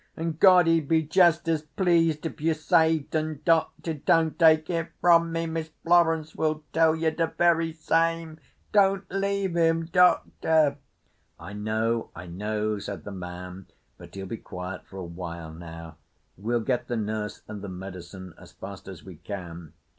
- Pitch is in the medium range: Yes, medium, 155 Hz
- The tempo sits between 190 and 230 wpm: No, average, 170 wpm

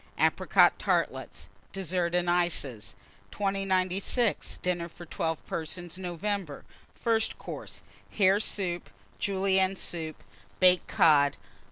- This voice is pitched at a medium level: Yes, medium, 180 Hz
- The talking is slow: Yes, slow, 95 wpm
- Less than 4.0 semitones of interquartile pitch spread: Yes, narrow, 2.4 semitones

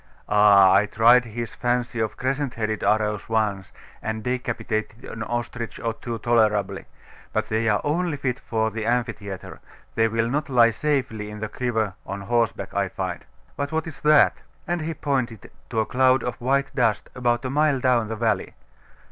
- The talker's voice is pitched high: No, low, 115 Hz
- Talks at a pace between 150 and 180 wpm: Yes, average, 175 wpm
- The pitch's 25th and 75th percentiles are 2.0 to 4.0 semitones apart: Yes, average, 2.8 semitones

